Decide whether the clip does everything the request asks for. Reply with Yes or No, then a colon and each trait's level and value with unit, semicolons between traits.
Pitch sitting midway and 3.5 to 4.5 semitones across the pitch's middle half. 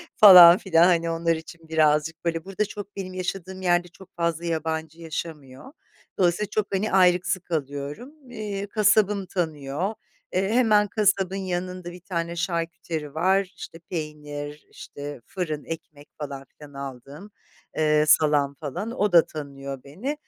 Yes: medium, 170 Hz; average, 3.9 semitones